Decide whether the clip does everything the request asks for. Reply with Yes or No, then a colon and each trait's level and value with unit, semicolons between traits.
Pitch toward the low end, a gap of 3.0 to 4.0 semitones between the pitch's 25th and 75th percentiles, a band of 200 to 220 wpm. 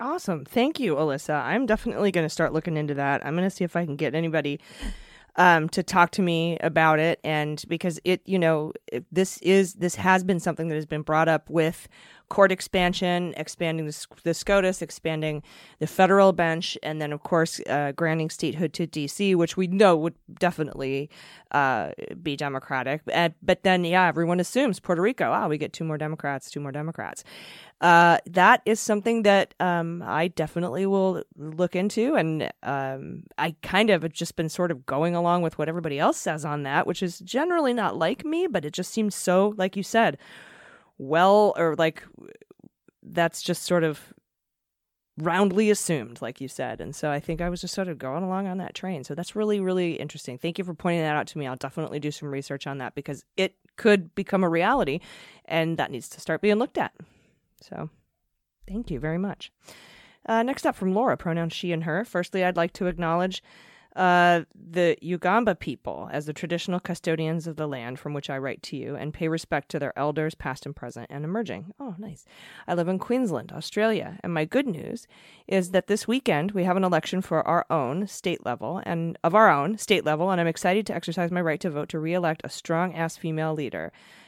No: medium, 170 Hz; average, 3.5 semitones; fast, 205 wpm